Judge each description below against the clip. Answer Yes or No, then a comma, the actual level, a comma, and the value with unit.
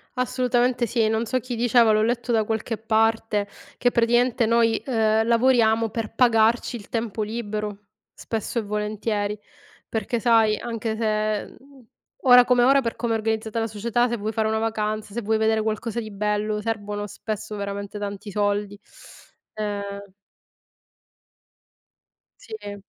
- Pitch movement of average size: No, narrow, 1.9 semitones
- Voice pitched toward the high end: Yes, high, 220 Hz